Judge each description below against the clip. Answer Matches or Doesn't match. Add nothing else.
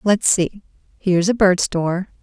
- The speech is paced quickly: Doesn't match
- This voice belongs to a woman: Matches